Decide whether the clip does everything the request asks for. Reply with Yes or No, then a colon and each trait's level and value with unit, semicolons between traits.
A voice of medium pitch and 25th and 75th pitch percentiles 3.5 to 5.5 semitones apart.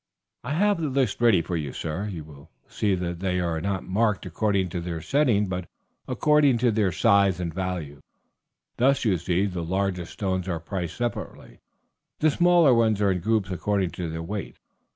No: very low, 95 Hz; average, 4.6 semitones